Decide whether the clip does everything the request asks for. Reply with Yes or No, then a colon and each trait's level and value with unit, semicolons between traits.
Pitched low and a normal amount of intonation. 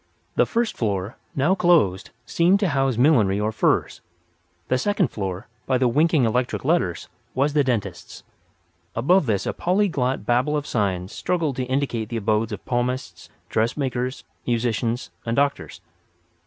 Yes: low, 125 Hz; average, 5.0 semitones